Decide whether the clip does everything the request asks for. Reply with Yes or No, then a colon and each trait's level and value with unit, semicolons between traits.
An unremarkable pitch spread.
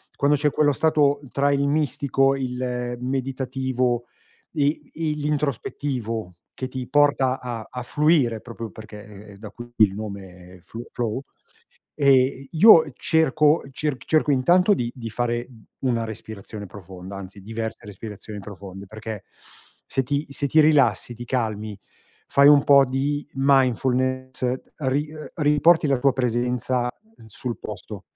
Yes: average, 4.0 semitones